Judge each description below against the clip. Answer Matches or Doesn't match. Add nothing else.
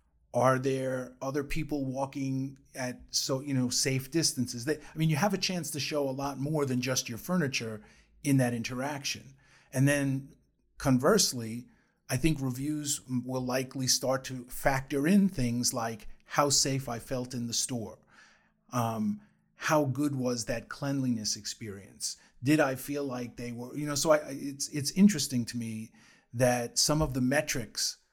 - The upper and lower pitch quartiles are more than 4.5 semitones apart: Doesn't match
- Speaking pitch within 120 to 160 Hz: Matches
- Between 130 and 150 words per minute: Doesn't match